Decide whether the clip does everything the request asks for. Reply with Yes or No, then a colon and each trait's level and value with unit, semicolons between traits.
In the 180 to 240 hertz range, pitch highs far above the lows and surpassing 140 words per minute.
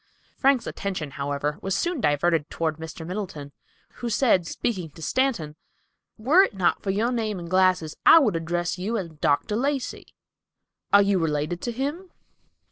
Yes: medium, 185 Hz; wide, 6.5 semitones; average, 160 wpm